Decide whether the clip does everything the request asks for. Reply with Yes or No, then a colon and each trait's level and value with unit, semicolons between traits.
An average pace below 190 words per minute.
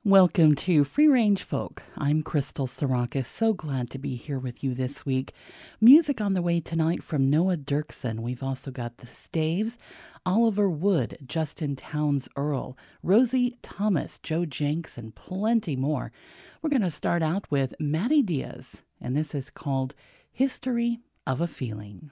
Yes: average, 155 wpm